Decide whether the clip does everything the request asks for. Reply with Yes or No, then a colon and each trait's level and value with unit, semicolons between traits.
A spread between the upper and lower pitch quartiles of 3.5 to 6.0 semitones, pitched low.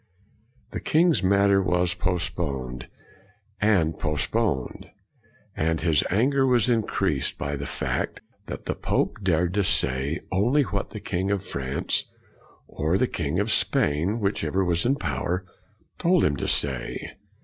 Yes: average, 5.1 semitones; very low, 90 Hz